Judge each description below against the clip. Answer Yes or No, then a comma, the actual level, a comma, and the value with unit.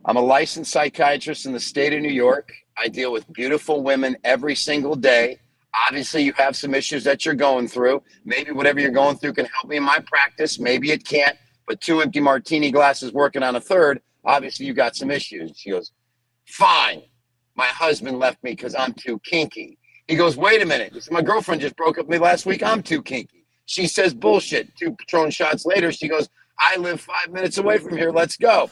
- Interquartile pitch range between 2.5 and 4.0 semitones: Yes, average, 3.7 semitones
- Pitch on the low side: No, medium, 145 Hz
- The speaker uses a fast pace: Yes, fast, 210 wpm